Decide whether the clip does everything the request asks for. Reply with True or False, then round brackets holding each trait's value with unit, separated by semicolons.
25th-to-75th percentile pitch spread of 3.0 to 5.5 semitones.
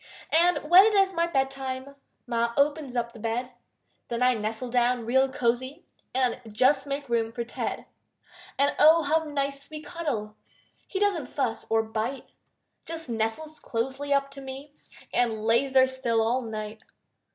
True (3.6 semitones)